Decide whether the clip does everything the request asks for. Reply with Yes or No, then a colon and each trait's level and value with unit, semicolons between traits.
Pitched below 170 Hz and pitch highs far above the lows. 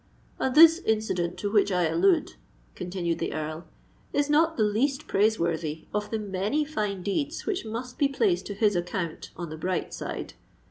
No: high, 210 Hz; wide, 8.2 semitones